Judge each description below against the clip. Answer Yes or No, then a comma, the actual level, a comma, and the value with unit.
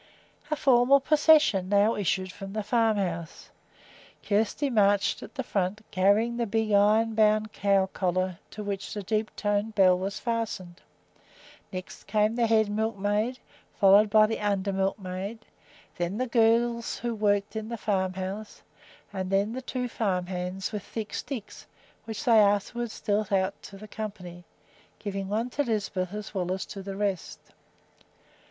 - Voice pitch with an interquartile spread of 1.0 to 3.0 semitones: Yes, narrow, 2.5 semitones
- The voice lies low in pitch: No, high, 205 Hz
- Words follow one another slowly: No, average, 155 wpm